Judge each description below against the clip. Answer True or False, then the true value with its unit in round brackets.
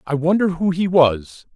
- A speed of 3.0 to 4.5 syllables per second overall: True (4.4 syllables/s)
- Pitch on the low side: False (165 Hz)